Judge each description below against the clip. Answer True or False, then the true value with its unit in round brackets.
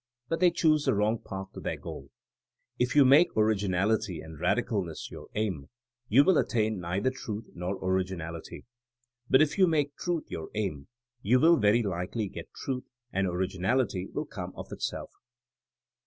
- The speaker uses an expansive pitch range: True (6.2 semitones)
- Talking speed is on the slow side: False (160 wpm)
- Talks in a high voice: False (105 Hz)